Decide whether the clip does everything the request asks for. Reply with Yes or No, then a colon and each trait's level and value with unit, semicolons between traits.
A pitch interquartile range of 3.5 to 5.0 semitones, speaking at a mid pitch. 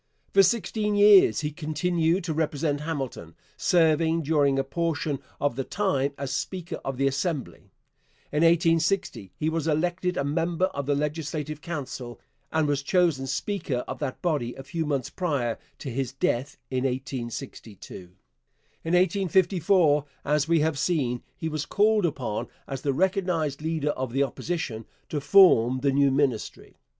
Yes: average, 3.9 semitones; medium, 150 Hz